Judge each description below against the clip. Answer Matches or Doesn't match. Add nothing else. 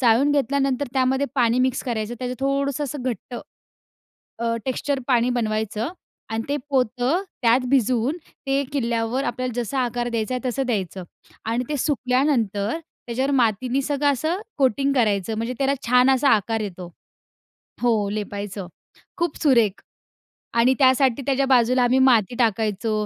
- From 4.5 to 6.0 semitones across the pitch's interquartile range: Doesn't match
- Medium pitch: Doesn't match